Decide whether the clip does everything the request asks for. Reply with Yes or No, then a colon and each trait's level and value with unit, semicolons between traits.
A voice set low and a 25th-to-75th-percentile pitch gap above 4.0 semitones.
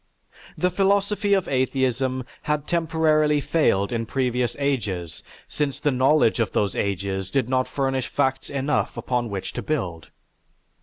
Yes: low, 130 Hz; average, 4.6 semitones